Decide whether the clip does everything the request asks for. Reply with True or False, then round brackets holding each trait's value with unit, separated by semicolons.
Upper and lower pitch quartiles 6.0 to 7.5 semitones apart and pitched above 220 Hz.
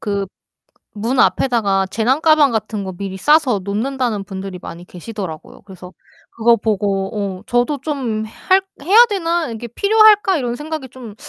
True (6.6 semitones; 230 Hz)